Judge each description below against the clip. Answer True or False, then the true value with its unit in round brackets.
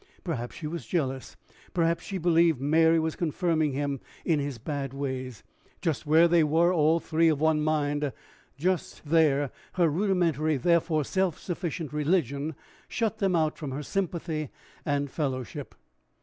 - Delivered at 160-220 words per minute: False (150 wpm)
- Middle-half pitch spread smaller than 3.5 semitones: True (2.8 semitones)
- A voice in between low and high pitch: True (155 Hz)